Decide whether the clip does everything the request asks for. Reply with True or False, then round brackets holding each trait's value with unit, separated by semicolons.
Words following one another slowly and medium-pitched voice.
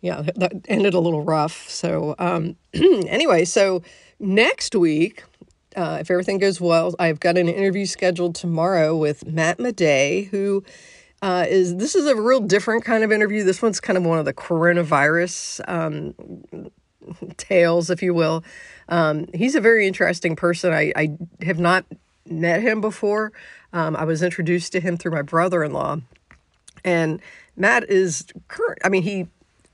False (165 wpm; 180 Hz)